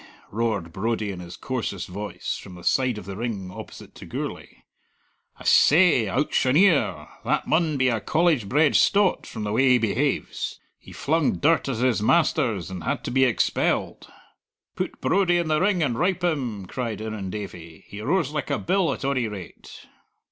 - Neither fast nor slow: Yes, average, 175 wpm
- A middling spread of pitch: No, wide, 6.9 semitones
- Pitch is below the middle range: Yes, low, 125 Hz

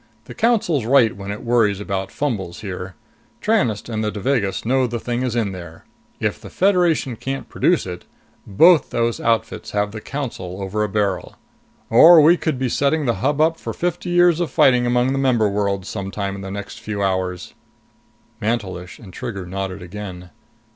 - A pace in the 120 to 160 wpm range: No, average, 180 wpm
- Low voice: Yes, low, 110 Hz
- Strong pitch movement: Yes, wide, 5.7 semitones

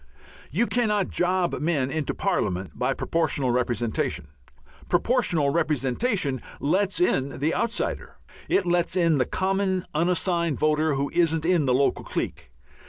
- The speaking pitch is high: No, medium, 165 Hz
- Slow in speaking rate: Yes, slow, 130 wpm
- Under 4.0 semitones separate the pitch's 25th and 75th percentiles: No, average, 4.7 semitones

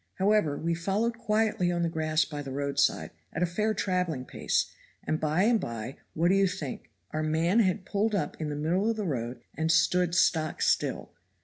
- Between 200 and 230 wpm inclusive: Yes, fast, 205 wpm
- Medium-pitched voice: Yes, medium, 170 Hz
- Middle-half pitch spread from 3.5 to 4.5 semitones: Yes, average, 4.2 semitones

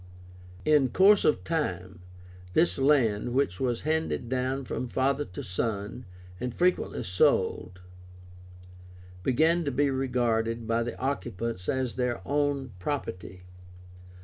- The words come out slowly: Yes, slow, 120 wpm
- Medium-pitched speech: No, low, 125 Hz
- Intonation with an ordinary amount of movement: Yes, average, 4.0 semitones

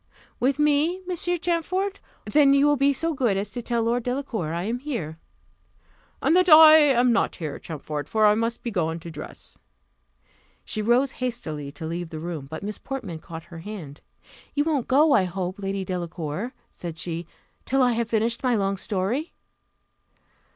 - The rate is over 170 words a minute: Yes, average, 180 wpm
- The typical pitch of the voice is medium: No, high, 225 Hz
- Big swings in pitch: Yes, wide, 8.2 semitones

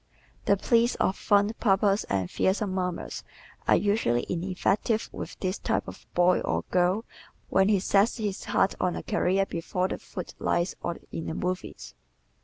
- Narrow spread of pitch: Yes, narrow, 2.2 semitones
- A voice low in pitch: No, high, 190 Hz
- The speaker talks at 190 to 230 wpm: No, average, 165 wpm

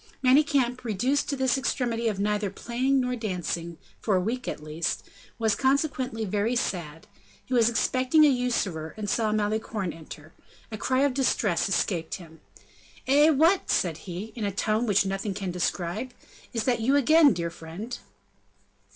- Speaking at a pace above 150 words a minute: Yes, average, 160 wpm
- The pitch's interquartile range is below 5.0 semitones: No, wide, 5.5 semitones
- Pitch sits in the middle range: No, high, 220 Hz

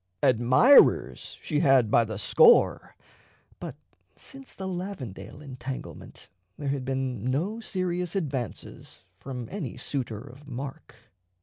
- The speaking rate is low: Yes, slow, 115 wpm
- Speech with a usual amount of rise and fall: No, wide, 6.4 semitones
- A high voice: No, low, 135 Hz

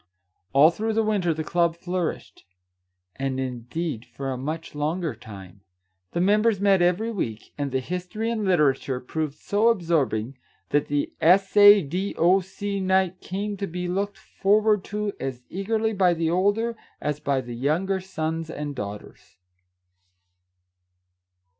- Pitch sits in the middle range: Yes, medium, 175 Hz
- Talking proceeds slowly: No, average, 145 wpm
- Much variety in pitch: Yes, wide, 5.7 semitones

